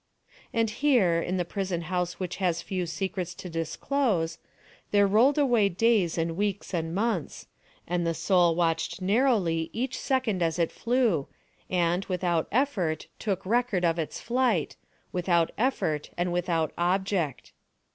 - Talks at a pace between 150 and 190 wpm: No, average, 140 wpm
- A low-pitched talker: No, medium, 180 Hz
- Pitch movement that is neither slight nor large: Yes, average, 4.4 semitones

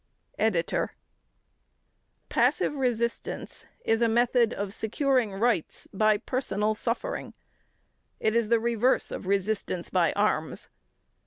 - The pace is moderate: No, slow, 105 wpm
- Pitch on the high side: Yes, high, 230 Hz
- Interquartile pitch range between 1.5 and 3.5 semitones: Yes, narrow, 2.5 semitones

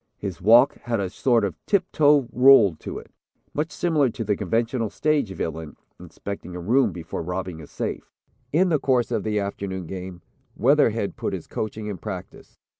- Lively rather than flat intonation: Yes, wide, 6.2 semitones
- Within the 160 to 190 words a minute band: Yes, average, 180 wpm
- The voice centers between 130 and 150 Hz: No, low, 105 Hz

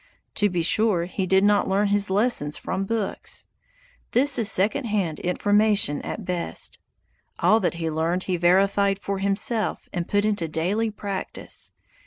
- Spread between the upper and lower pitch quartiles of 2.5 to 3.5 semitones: Yes, average, 2.9 semitones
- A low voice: No, high, 195 Hz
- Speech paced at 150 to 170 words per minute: Yes, average, 155 wpm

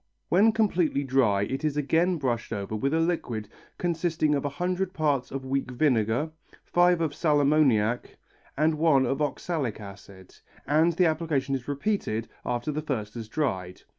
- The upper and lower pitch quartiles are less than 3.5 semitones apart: No, average, 5.1 semitones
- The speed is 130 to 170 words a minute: Yes, average, 165 wpm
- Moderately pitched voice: Yes, medium, 145 Hz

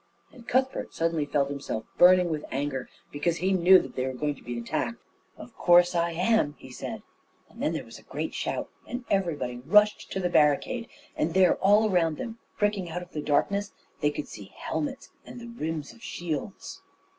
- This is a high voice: No, medium, 175 Hz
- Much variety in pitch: Yes, wide, 5.8 semitones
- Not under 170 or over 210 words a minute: Yes, average, 195 wpm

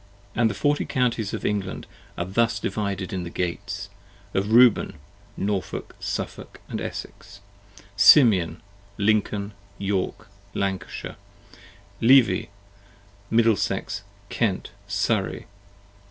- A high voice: No, low, 100 Hz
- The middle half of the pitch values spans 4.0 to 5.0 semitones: No, average, 2.9 semitones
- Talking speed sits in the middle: No, slow, 95 wpm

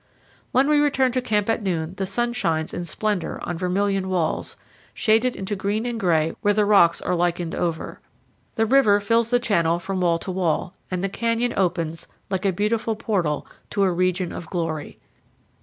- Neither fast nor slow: Yes, average, 185 wpm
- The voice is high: Yes, high, 195 Hz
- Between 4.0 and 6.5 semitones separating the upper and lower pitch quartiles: Yes, average, 4.4 semitones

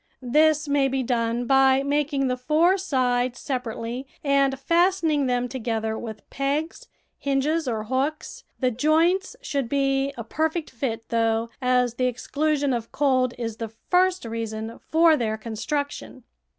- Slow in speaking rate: No, average, 145 wpm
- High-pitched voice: Yes, very high, 265 Hz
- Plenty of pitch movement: No, average, 4.0 semitones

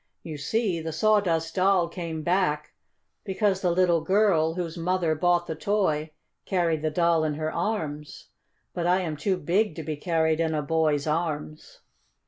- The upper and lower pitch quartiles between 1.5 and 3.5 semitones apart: Yes, average, 2.8 semitones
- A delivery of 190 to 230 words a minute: No, average, 165 wpm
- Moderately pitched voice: Yes, medium, 165 Hz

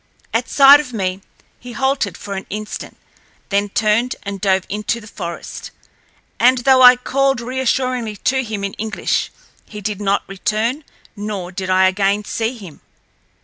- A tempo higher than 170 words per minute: No, average, 155 wpm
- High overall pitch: Yes, high, 215 Hz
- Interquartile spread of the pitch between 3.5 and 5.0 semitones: Yes, average, 4.0 semitones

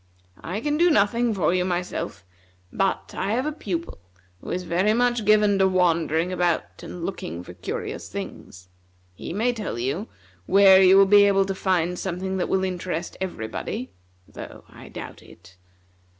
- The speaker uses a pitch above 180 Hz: Yes, high, 190 Hz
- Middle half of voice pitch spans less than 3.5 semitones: Yes, average, 2.9 semitones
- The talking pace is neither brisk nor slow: Yes, average, 165 wpm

